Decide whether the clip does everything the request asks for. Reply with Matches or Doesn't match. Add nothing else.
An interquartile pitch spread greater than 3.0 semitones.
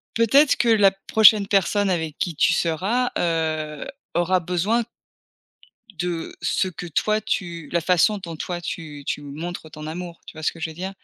Matches